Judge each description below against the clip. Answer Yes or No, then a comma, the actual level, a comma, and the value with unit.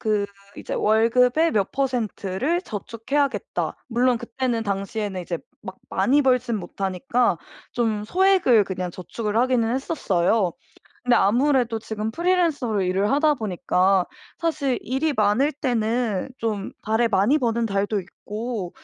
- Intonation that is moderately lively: Yes, average, 4.3 semitones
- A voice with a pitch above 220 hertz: Yes, high, 230 Hz